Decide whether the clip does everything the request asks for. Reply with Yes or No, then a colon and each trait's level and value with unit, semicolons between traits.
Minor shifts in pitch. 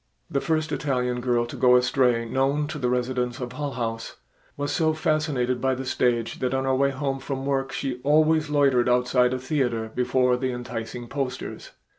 Yes: narrow, 2.1 semitones